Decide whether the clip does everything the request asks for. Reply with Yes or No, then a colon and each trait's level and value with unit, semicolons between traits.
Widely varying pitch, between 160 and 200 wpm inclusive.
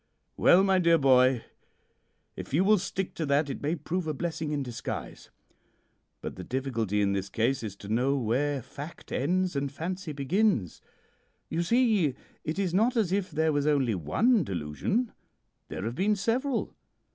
Yes: wide, 6.6 semitones; average, 170 wpm